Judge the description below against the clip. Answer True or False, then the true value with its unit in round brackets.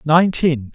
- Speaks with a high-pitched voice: False (155 Hz)